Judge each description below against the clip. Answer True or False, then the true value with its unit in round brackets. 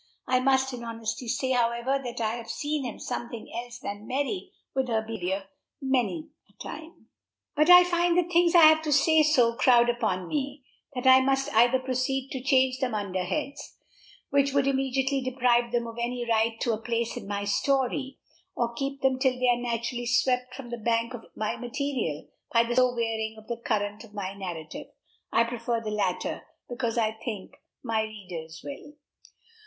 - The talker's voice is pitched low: False (245 Hz)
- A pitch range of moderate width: True (3.0 semitones)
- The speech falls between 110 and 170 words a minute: False (185 wpm)